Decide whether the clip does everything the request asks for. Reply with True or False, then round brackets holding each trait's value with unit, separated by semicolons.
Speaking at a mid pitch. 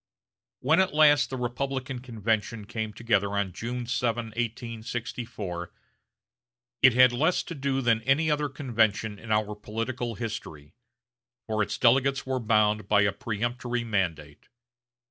False (115 Hz)